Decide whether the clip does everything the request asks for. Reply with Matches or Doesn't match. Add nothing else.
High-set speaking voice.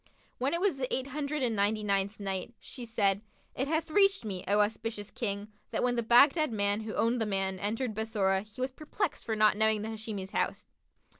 Matches